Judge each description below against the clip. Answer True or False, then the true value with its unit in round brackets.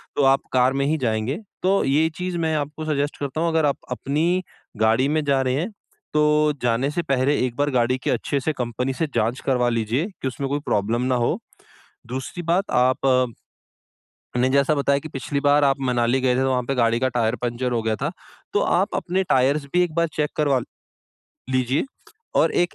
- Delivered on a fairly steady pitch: False (3.3 semitones)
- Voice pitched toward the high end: False (135 Hz)